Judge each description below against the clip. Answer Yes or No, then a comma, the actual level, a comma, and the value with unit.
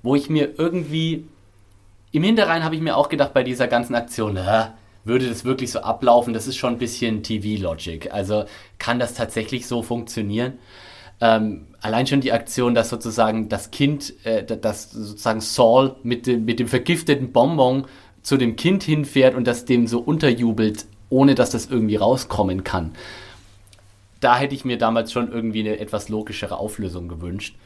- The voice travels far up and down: No, average, 3.4 semitones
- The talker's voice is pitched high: No, low, 115 Hz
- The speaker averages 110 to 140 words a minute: No, average, 170 wpm